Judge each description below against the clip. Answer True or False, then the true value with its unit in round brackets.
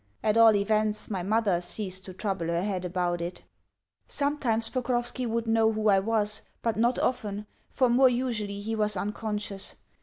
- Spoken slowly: False (170 wpm)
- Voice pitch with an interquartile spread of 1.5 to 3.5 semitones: True (2.5 semitones)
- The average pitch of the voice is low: False (215 Hz)